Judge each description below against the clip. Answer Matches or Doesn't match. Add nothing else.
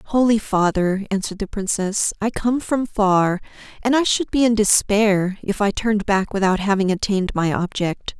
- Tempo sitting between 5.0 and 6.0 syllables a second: Doesn't match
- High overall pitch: Matches